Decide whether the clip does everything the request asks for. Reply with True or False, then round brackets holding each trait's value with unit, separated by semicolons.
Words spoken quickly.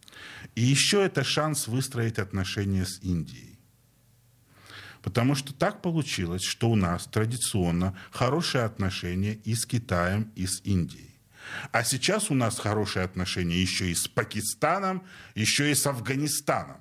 False (135 wpm)